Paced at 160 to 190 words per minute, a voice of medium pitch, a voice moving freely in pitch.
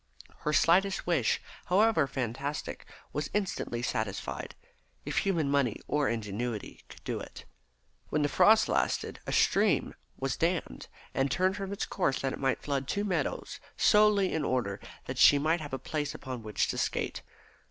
Yes: average, 165 wpm; medium, 145 Hz; wide, 6.3 semitones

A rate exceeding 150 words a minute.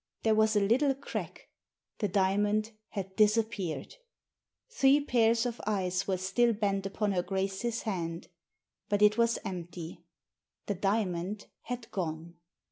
No: slow, 135 wpm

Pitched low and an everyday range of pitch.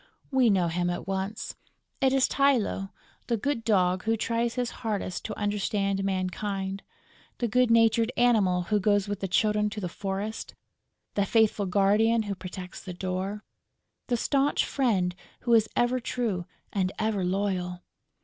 No: high, 205 Hz; average, 3.2 semitones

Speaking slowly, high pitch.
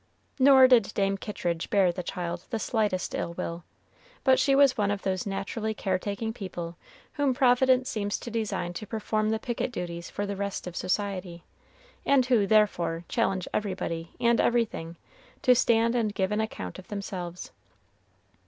No: average, 165 wpm; high, 205 Hz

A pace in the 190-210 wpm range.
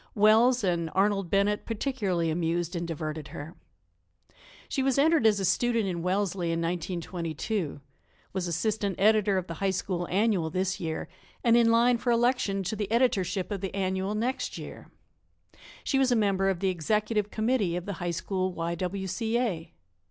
No: average, 175 wpm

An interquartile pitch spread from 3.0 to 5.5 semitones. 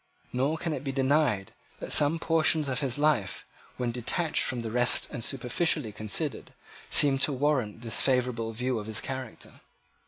Yes: average, 4.1 semitones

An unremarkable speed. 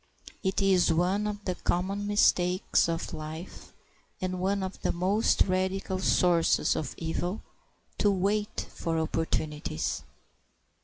No: slow, 120 wpm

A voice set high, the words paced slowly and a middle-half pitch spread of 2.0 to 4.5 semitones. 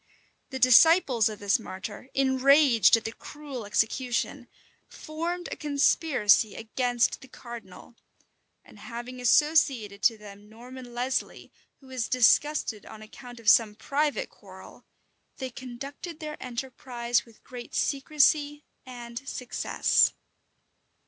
Yes: very high, 250 Hz; slow, 115 wpm; average, 3.5 semitones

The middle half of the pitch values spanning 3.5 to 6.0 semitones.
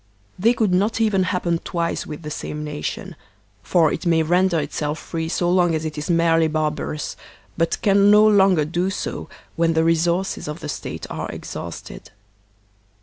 No: average, 3.0 semitones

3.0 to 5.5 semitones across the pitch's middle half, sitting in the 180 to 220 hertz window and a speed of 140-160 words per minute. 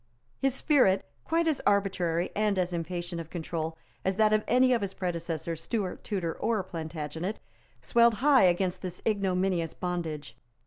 Yes: average, 4.1 semitones; medium, 185 Hz; average, 150 wpm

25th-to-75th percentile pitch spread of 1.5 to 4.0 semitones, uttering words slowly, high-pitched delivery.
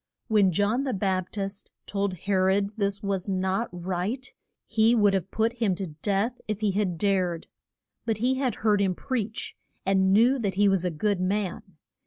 No: narrow, 2.5 semitones; average, 185 wpm; high, 200 Hz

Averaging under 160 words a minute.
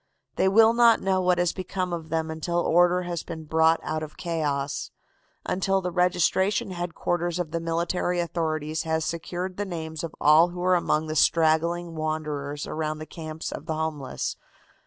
No: average, 175 wpm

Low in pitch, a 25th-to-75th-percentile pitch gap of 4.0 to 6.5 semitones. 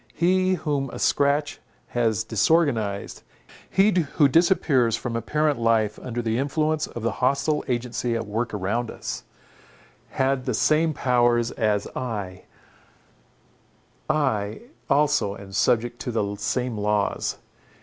Yes: low, 120 Hz; average, 4.9 semitones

